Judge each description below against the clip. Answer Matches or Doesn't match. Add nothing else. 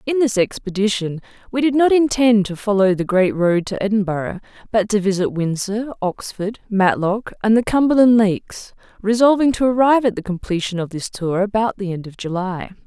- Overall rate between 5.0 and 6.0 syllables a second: Matches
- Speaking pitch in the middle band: Doesn't match